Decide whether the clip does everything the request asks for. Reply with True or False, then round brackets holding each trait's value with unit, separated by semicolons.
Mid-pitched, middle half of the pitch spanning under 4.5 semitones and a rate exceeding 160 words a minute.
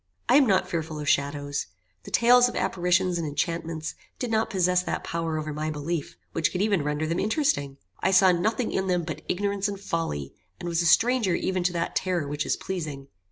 True (175 Hz; 3.7 semitones; 205 wpm)